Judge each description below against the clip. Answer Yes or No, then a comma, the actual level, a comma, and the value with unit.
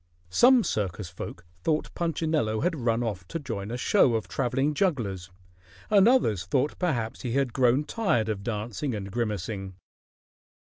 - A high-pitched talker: No, low, 120 Hz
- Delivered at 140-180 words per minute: Yes, average, 150 wpm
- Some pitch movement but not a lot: No, wide, 6.5 semitones